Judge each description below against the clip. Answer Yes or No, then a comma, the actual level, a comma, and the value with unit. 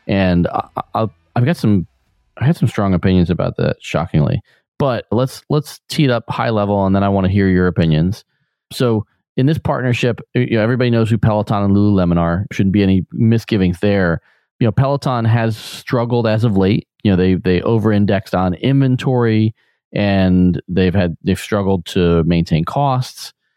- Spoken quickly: No, average, 180 wpm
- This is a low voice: Yes, low, 105 Hz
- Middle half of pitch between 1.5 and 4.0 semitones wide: No, average, 4.6 semitones